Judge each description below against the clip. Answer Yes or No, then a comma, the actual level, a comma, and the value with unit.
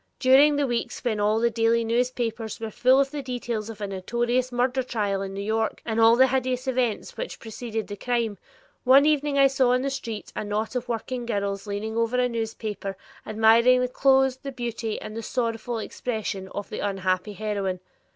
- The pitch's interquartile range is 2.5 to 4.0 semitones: Yes, average, 2.9 semitones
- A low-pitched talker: No, high, 230 Hz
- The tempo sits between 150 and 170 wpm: No, average, 190 wpm